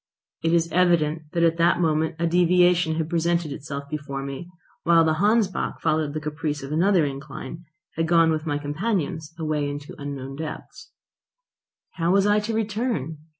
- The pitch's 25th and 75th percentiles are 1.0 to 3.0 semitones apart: Yes, narrow, 2.6 semitones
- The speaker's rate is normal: Yes, average, 165 wpm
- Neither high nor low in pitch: Yes, medium, 160 Hz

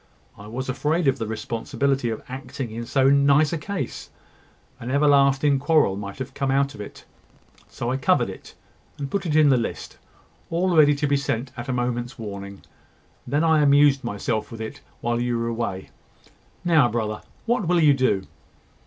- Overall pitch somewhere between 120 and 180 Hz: Yes, low, 135 Hz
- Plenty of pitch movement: No, average, 3.9 semitones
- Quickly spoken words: No, average, 180 wpm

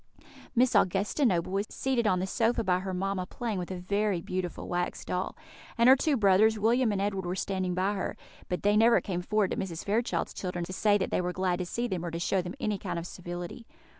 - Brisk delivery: Yes, fast, 235 wpm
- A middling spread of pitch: Yes, average, 3.2 semitones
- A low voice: No, high, 190 Hz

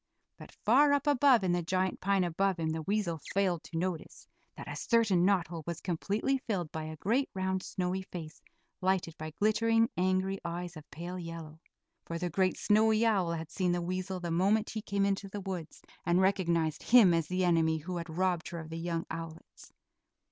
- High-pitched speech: No, medium, 180 Hz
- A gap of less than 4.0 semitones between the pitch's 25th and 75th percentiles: Yes, average, 3.0 semitones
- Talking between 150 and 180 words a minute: No, average, 200 wpm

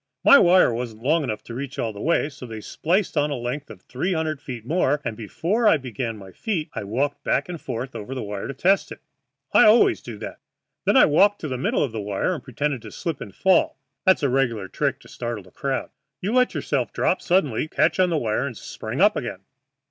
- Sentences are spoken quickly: Yes, fast, 235 wpm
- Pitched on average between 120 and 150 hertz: Yes, low, 135 Hz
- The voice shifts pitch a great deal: Yes, wide, 6.4 semitones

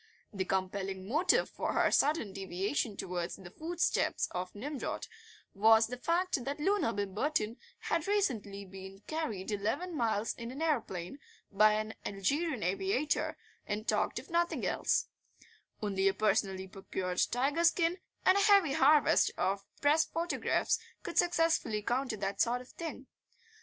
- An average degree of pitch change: No, wide, 8.0 semitones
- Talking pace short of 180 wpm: Yes, average, 140 wpm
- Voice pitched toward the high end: Yes, high, 225 Hz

